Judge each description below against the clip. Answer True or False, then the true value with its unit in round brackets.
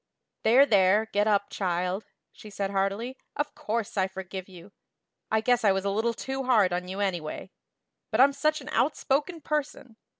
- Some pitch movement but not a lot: True (4.9 semitones)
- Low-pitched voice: False (210 Hz)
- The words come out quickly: False (175 wpm)